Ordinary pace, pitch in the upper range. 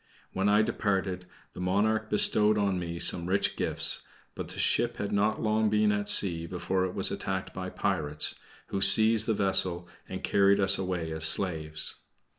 No: average, 175 wpm; very low, 95 Hz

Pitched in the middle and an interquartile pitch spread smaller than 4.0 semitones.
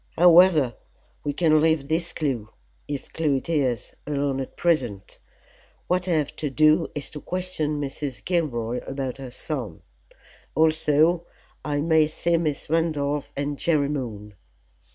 Yes: medium, 150 Hz; average, 2.9 semitones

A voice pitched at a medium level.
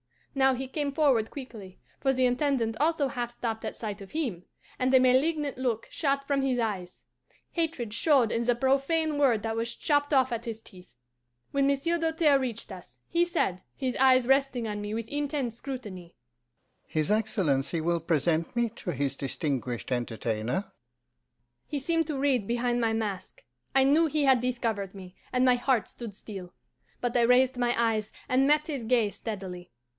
No: high, 245 Hz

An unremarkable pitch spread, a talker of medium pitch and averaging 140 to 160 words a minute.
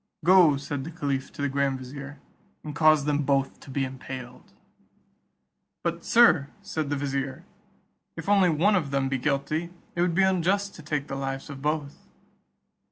No: average, 3.4 semitones; medium, 145 Hz; average, 170 wpm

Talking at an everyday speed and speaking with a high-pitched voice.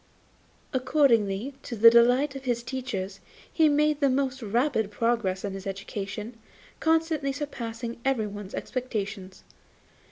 No: slow, 120 wpm; high, 235 Hz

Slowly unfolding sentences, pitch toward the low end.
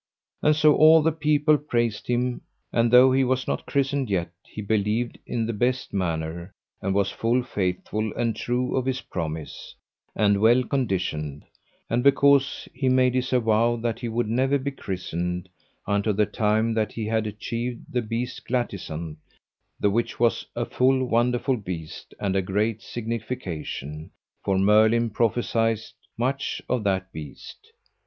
No: average, 155 wpm; low, 115 Hz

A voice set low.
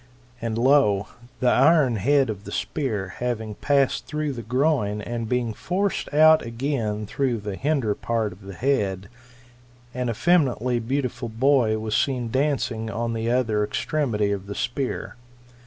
Yes: low, 120 Hz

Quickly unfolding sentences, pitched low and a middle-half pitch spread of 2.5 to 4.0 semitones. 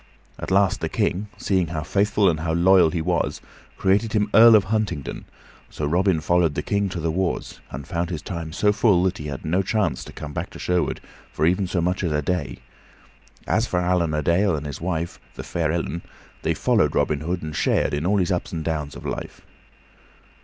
Yes: fast, 215 wpm; very low, 85 Hz; average, 3.4 semitones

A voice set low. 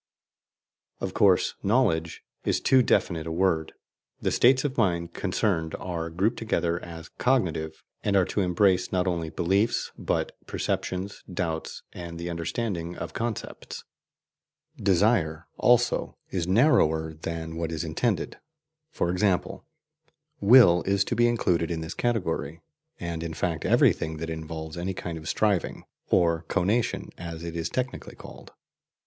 Yes: very low, 85 Hz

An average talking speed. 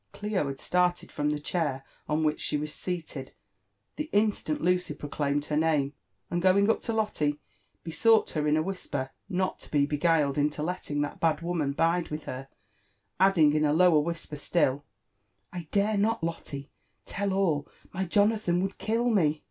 Yes: average, 180 wpm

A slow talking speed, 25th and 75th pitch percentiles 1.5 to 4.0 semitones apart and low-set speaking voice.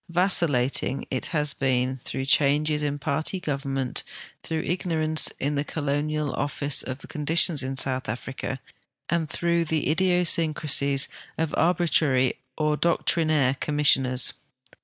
No: slow, 115 wpm; average, 2.9 semitones; medium, 150 Hz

